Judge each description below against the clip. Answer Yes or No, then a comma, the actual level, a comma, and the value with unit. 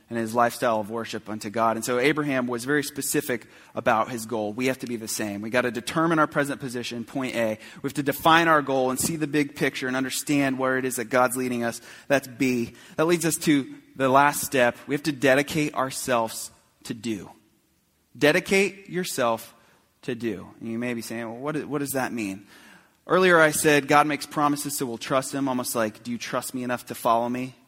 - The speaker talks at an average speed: No, fast, 225 wpm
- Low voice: Yes, low, 130 Hz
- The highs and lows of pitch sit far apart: No, average, 4.0 semitones